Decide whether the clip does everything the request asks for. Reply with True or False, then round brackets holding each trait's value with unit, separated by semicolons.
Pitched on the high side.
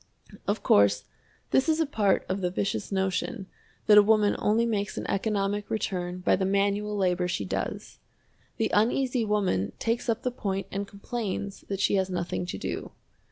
True (200 Hz)